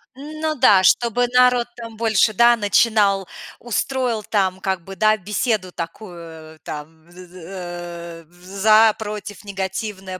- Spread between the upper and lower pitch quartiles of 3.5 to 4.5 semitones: Yes, average, 4.1 semitones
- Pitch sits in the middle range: No, high, 200 Hz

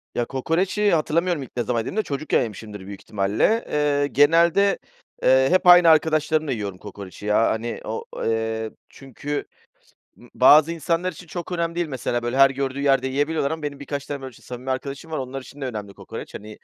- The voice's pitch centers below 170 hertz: Yes, medium, 140 Hz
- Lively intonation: No, average, 5.0 semitones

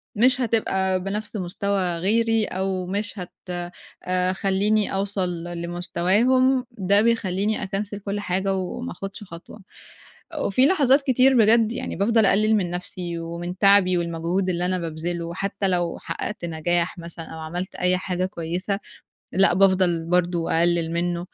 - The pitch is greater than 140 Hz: Yes, medium, 185 Hz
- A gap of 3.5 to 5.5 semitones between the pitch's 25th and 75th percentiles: No, average, 2.9 semitones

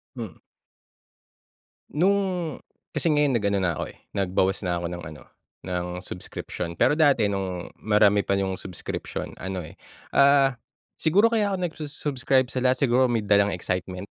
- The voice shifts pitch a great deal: Yes, wide, 7.6 semitones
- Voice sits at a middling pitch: No, low, 105 Hz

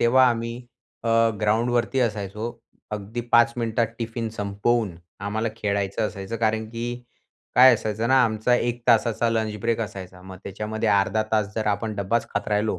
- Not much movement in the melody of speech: Yes, narrow, 2.1 semitones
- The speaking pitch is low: Yes, low, 110 Hz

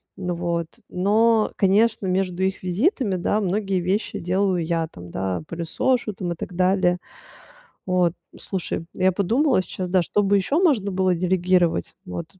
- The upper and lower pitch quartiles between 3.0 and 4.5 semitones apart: No, narrow, 2.4 semitones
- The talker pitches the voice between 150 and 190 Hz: Yes, medium, 185 Hz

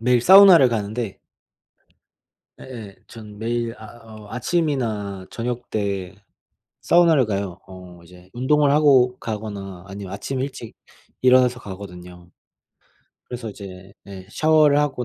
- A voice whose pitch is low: Yes, low, 110 Hz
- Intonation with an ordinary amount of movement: Yes, average, 4.7 semitones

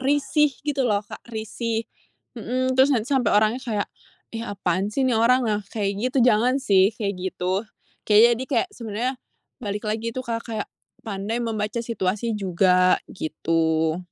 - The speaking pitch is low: No, high, 220 Hz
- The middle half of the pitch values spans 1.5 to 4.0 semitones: Yes, average, 3.4 semitones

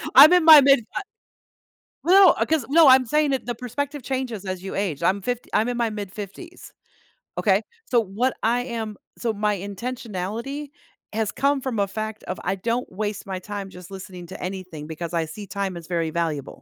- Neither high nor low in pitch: No, high, 215 Hz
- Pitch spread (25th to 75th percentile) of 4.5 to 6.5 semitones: Yes, average, 5.3 semitones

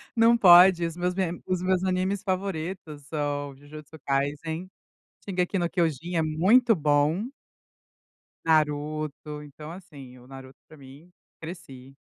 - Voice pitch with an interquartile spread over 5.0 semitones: No, average, 4.0 semitones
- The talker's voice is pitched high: No, medium, 160 Hz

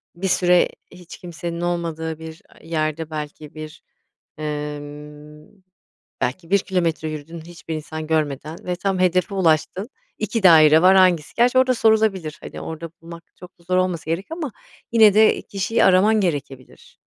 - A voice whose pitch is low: No, medium, 170 Hz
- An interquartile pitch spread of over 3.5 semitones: No, average, 3.2 semitones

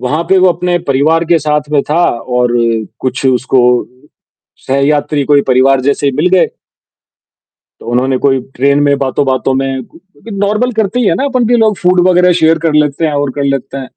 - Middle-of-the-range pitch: Yes, medium, 145 Hz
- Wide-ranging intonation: No, average, 4.7 semitones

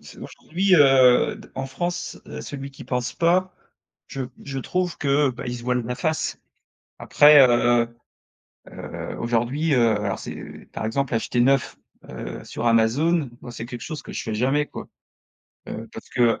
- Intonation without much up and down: No, average, 3.6 semitones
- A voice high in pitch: No, low, 130 Hz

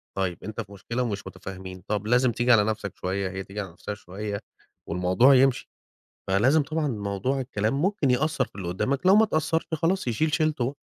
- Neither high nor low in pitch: No, low, 115 Hz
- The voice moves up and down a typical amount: No, wide, 6.0 semitones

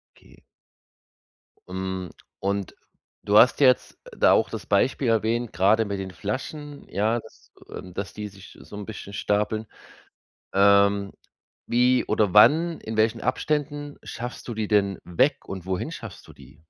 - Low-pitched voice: Yes, low, 105 Hz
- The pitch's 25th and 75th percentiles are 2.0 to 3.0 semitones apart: No, average, 3.7 semitones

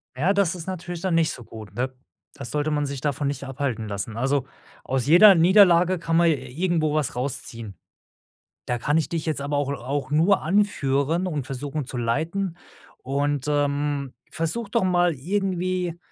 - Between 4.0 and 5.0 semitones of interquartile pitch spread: Yes, average, 4.5 semitones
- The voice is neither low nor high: Yes, medium, 150 Hz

